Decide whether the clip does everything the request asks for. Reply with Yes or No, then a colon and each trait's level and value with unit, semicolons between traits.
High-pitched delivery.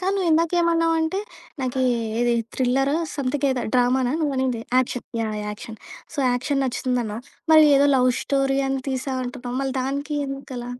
Yes: very high, 265 Hz